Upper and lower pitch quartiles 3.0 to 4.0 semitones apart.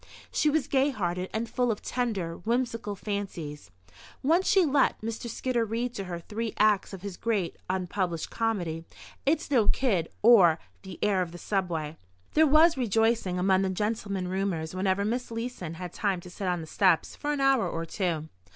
No: average, 4.8 semitones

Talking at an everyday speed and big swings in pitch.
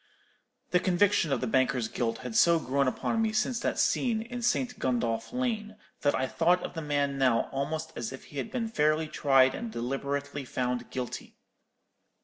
Yes: average, 180 wpm; wide, 7.9 semitones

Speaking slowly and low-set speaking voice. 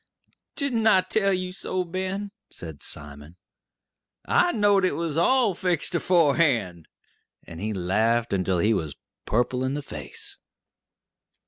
No: slow, 130 wpm; medium, 155 Hz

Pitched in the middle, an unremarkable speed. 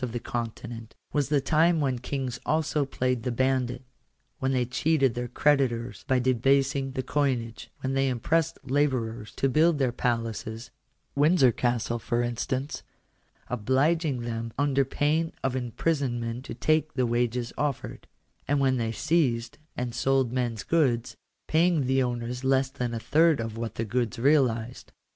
No: low, 130 Hz; average, 155 wpm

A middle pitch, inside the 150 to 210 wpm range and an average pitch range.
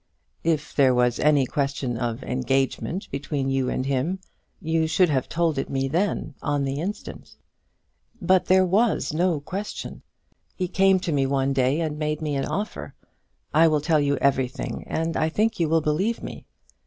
Yes: medium, 150 Hz; average, 175 wpm; average, 4.1 semitones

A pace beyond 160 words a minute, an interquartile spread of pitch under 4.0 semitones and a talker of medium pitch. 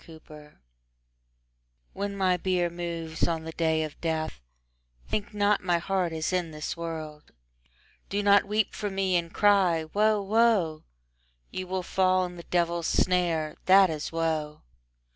No: average, 145 wpm; average, 3.2 semitones; medium, 175 Hz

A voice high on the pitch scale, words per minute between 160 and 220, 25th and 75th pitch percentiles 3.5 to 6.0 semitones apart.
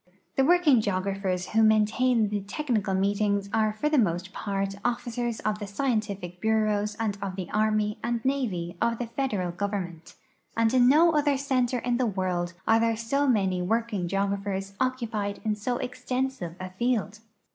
Yes: high, 215 Hz; average, 170 wpm; average, 3.8 semitones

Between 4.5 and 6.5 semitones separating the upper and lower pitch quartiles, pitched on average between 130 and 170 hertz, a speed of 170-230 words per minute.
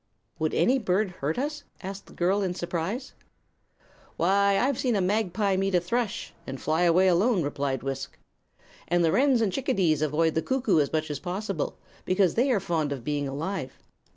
No: average, 5.2 semitones; medium, 185 Hz; average, 180 wpm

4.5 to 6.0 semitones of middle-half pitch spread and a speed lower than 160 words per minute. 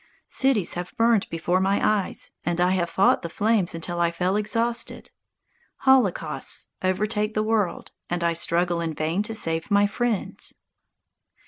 No: average, 3.8 semitones; average, 150 wpm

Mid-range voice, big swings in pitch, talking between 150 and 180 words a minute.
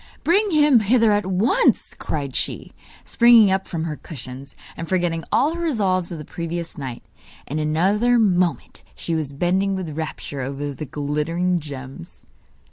Yes: medium, 175 Hz; wide, 5.7 semitones; average, 155 wpm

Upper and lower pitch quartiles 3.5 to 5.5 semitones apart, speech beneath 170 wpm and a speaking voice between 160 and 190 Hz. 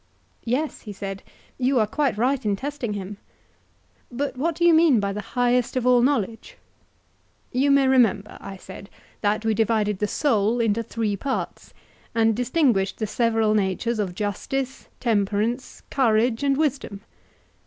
No: average, 4.1 semitones; average, 155 wpm; high, 230 Hz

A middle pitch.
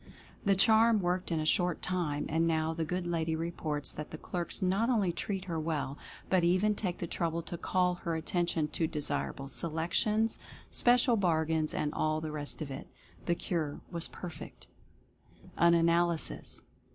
Yes: medium, 170 Hz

